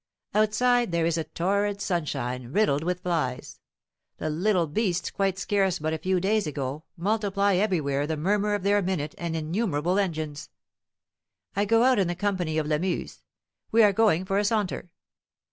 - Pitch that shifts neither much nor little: Yes, average, 4.5 semitones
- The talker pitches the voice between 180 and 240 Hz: Yes, medium, 185 Hz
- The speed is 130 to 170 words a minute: Yes, average, 160 wpm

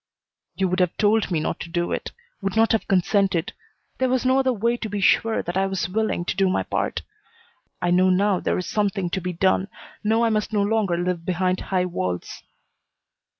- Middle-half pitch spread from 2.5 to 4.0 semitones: Yes, average, 3.2 semitones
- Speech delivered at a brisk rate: Yes, fast, 210 wpm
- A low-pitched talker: No, high, 195 Hz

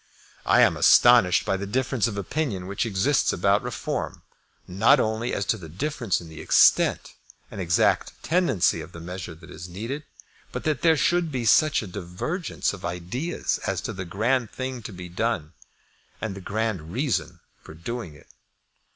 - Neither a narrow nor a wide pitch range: No, wide, 6.4 semitones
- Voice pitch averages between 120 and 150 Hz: No, low, 105 Hz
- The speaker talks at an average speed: Yes, average, 175 wpm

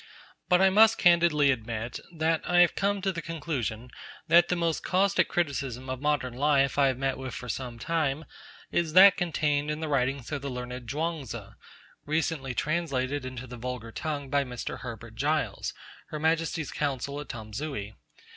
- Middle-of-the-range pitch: Yes, medium, 145 Hz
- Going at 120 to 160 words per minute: No, average, 175 wpm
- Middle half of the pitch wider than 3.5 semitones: Yes, average, 4.4 semitones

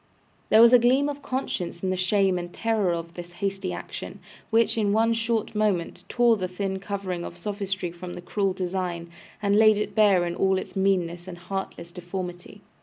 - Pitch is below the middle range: No, high, 190 Hz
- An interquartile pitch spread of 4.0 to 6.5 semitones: No, average, 3.2 semitones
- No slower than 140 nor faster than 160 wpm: No, average, 190 wpm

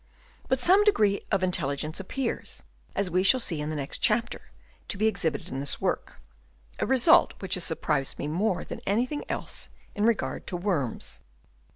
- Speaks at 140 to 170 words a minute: No, average, 185 wpm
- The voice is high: Yes, high, 195 Hz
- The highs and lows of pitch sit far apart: Yes, wide, 6.7 semitones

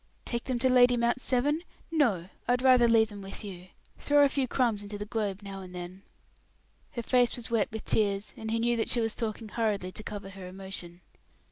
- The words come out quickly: Yes, fast, 220 wpm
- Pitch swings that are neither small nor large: Yes, average, 3.7 semitones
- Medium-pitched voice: No, high, 220 Hz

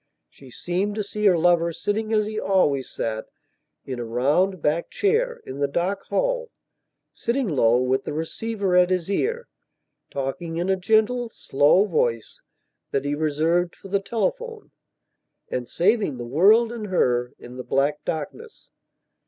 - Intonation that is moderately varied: No, wide, 7.1 semitones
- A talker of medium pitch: Yes, medium, 180 Hz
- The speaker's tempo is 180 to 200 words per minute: No, average, 150 wpm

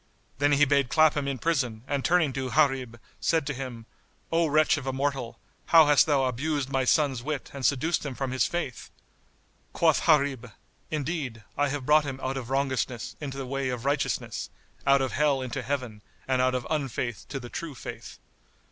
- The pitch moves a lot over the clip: No, narrow, 2.4 semitones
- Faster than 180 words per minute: Yes, average, 190 wpm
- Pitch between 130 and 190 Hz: Yes, low, 135 Hz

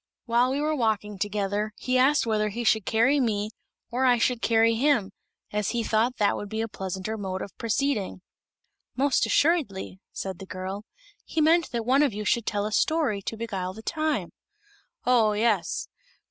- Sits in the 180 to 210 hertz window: No, high, 225 Hz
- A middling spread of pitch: Yes, average, 3.7 semitones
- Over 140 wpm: Yes, average, 180 wpm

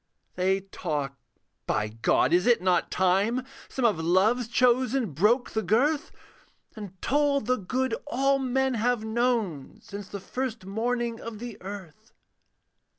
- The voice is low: No, high, 220 Hz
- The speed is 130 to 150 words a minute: Yes, average, 140 wpm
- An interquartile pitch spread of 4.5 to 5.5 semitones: Yes, average, 5.0 semitones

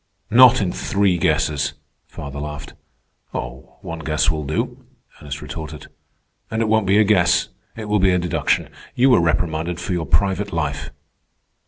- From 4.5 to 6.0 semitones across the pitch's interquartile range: Yes, average, 4.8 semitones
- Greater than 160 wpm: No, average, 155 wpm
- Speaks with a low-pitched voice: Yes, very low, 85 Hz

